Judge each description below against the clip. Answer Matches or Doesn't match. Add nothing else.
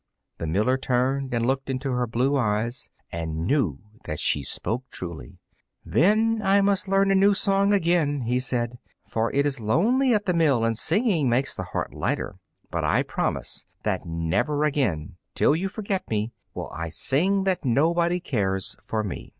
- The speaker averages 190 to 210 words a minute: Doesn't match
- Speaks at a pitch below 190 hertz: Matches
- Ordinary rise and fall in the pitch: Doesn't match